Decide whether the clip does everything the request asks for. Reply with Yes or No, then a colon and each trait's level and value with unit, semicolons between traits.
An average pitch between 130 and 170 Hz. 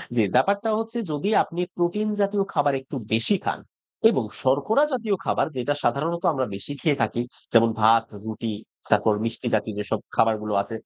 Yes: medium, 140 Hz